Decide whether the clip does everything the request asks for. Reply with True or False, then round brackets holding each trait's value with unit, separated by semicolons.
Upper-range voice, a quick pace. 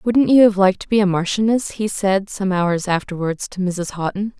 True (195 Hz; 220 wpm)